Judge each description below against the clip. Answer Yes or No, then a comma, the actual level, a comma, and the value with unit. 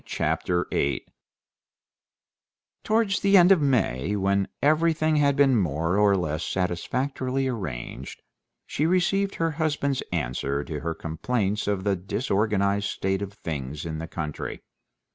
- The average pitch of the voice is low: Yes, low, 100 Hz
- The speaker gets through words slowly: Yes, slow, 130 wpm